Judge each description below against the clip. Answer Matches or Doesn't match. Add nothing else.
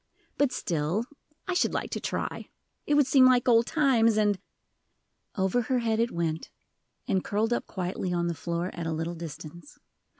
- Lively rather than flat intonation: Matches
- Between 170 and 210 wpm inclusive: Matches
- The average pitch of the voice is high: Matches